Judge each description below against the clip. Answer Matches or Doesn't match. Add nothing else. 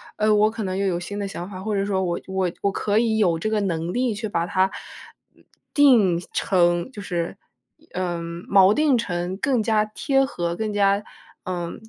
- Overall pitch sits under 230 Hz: Matches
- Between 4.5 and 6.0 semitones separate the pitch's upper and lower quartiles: Doesn't match